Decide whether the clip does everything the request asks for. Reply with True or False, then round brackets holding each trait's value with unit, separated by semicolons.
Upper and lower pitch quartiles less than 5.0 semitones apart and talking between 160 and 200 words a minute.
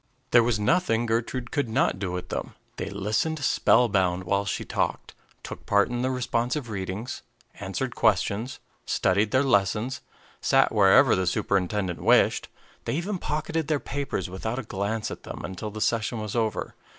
True (4.2 semitones; 165 wpm)